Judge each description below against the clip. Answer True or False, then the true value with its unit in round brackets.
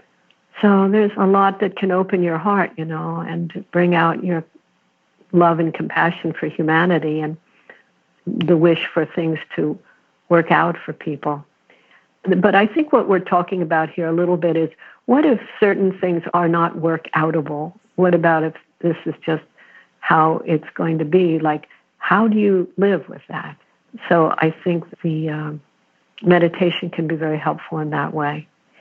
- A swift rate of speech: False (170 wpm)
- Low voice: False (170 Hz)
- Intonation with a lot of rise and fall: False (2.5 semitones)